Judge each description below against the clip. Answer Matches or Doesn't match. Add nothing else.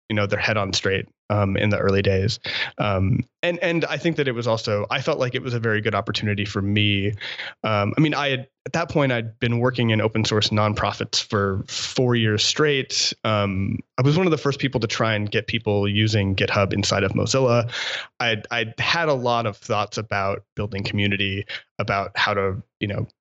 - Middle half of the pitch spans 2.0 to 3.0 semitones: Doesn't match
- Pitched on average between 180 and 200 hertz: Doesn't match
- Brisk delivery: Matches